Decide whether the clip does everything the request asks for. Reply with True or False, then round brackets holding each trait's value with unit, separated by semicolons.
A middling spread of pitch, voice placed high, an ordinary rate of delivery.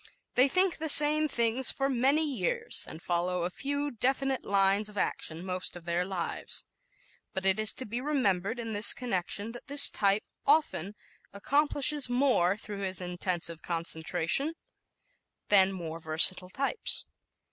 False (7.0 semitones; 210 Hz; 145 wpm)